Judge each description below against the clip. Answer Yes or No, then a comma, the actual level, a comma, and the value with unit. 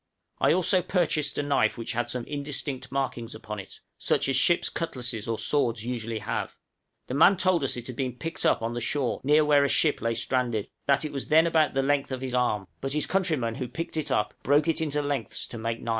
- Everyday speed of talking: No, fast, 235 wpm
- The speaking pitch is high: No, low, 135 Hz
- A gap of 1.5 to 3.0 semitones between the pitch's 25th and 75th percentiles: No, average, 4.1 semitones